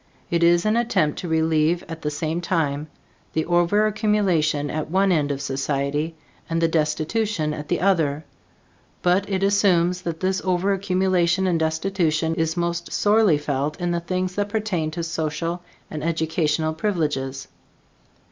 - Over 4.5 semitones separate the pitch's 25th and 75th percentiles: No, average, 3.2 semitones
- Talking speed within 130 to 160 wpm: Yes, average, 145 wpm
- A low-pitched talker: No, medium, 170 Hz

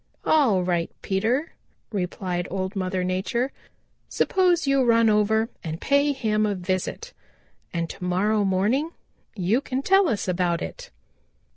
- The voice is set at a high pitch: Yes, high, 210 Hz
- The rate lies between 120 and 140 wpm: Yes, slow, 135 wpm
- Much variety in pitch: Yes, wide, 6.1 semitones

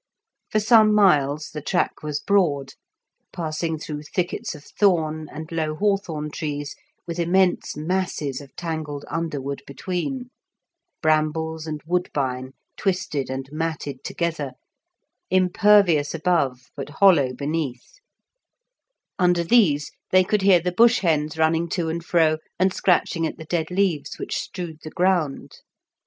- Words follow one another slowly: Yes, slow, 130 wpm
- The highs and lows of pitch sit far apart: No, average, 3.3 semitones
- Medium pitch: Yes, medium, 160 Hz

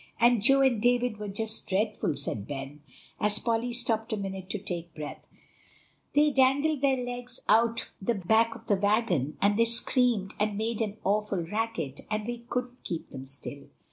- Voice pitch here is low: No, high, 220 Hz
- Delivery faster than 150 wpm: Yes, average, 170 wpm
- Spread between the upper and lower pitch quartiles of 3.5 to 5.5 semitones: Yes, average, 3.9 semitones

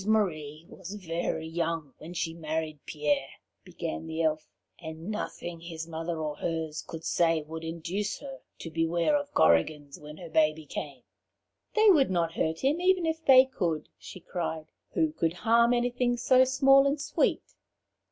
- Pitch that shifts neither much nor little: No, wide, 6.8 semitones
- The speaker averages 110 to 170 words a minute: Yes, average, 165 wpm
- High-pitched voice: No, medium, 165 Hz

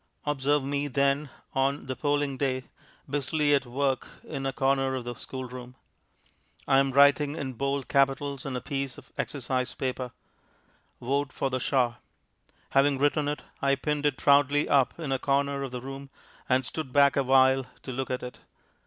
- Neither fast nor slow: Yes, average, 170 wpm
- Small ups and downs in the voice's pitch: Yes, narrow, 1.4 semitones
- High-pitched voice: No, low, 135 Hz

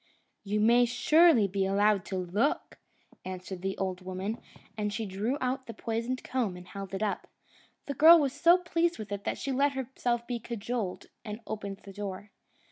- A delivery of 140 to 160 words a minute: No, average, 185 wpm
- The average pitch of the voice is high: Yes, high, 215 Hz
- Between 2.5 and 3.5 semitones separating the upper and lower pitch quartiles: No, average, 4.6 semitones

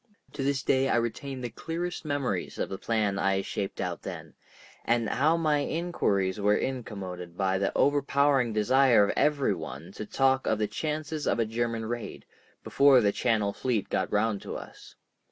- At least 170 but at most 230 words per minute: Yes, average, 175 wpm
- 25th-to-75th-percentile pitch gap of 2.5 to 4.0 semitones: No, wide, 5.4 semitones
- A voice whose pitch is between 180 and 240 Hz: No, low, 120 Hz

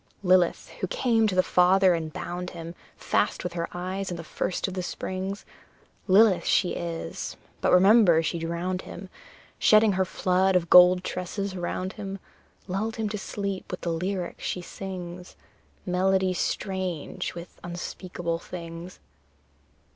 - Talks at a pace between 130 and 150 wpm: Yes, average, 145 wpm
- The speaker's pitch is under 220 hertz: Yes, medium, 185 Hz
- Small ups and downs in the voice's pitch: Yes, narrow, 1.8 semitones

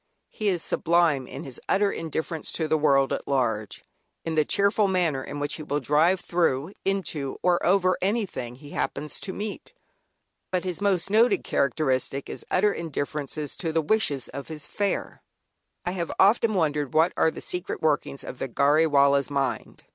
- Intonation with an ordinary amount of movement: Yes, average, 4.7 semitones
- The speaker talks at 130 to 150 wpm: No, average, 175 wpm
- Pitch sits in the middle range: Yes, medium, 160 Hz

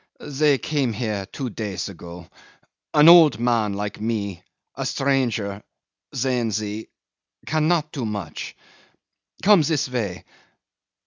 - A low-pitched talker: Yes, low, 115 Hz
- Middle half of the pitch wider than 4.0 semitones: Yes, wide, 5.4 semitones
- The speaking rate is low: Yes, slow, 115 wpm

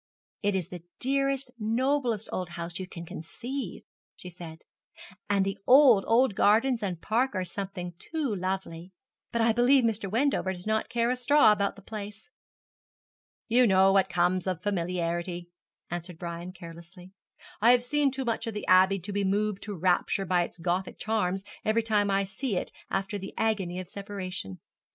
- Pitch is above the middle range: Yes, high, 195 Hz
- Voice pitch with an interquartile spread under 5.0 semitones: Yes, average, 4.0 semitones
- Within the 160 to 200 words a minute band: Yes, average, 175 wpm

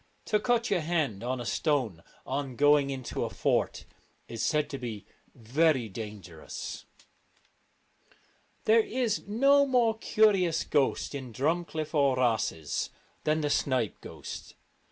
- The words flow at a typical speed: No, slow, 130 wpm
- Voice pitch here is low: No, medium, 145 Hz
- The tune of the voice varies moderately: No, wide, 6.9 semitones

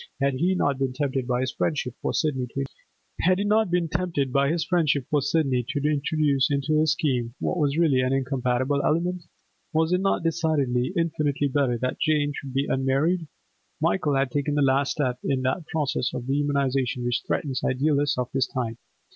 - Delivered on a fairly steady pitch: No, average, 3.2 semitones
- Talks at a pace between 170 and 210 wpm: No, average, 155 wpm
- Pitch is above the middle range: No, medium, 140 Hz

